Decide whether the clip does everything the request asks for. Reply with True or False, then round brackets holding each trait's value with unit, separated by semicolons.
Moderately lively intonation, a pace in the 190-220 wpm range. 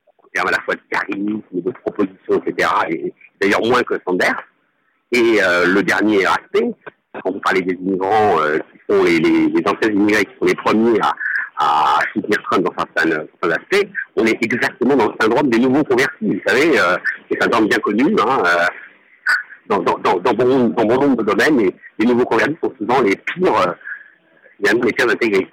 True (3.3 semitones; 195 wpm)